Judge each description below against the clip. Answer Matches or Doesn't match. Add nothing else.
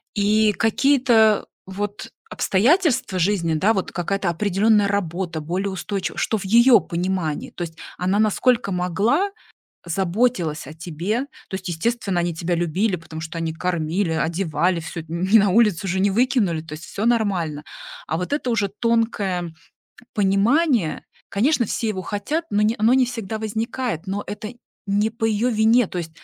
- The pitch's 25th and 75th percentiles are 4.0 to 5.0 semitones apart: Matches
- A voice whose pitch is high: Matches